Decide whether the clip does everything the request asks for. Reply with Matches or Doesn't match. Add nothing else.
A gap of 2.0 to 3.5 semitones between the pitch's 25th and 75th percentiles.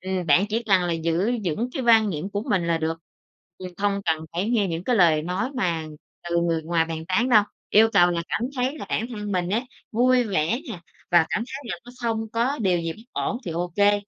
Doesn't match